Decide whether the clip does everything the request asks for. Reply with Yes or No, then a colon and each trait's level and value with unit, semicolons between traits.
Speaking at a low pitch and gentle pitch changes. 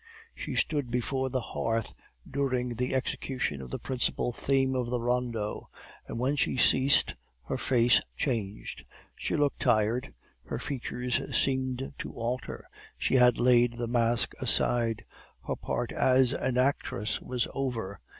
Yes: low, 125 Hz; narrow, 2.0 semitones